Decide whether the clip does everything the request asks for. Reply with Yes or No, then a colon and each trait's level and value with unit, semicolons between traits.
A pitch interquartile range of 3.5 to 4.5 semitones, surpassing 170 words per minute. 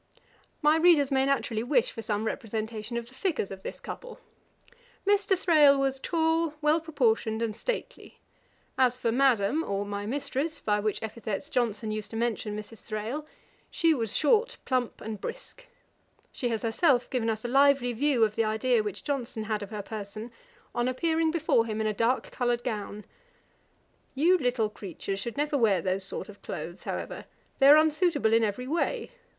No: average, 5.3 semitones; average, 180 wpm